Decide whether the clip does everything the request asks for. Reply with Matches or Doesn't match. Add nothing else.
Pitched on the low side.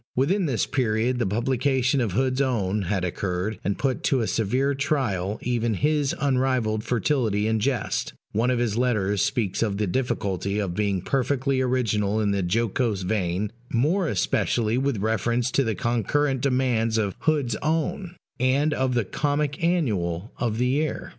Matches